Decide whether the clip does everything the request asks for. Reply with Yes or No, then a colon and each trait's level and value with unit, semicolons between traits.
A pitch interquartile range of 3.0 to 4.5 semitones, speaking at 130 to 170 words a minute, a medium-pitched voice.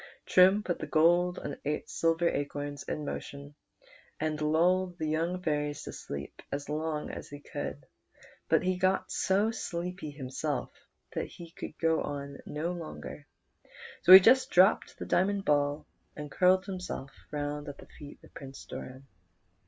Yes: average, 3.8 semitones; average, 155 wpm; medium, 155 Hz